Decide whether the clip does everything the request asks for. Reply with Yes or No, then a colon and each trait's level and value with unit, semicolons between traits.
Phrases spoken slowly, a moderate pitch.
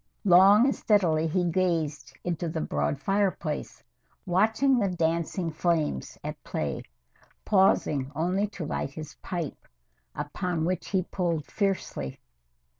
Yes: slow, 120 wpm; medium, 175 Hz